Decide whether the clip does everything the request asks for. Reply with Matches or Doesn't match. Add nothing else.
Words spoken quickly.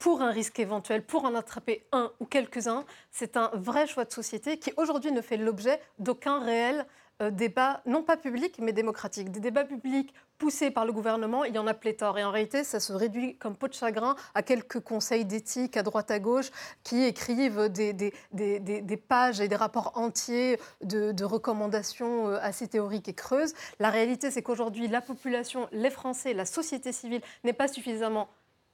Doesn't match